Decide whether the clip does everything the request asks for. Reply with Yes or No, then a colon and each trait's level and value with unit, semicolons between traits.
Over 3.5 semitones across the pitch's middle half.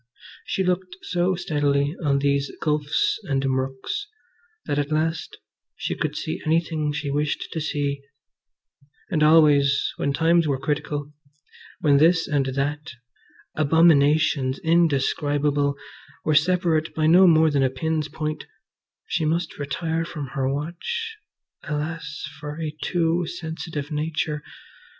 No: narrow, 2.4 semitones